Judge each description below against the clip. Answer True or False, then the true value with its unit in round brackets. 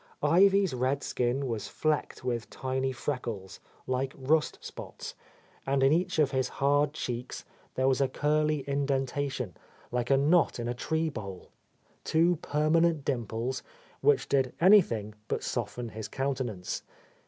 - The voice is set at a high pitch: False (135 Hz)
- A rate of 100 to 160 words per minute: True (145 wpm)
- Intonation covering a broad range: False (3.7 semitones)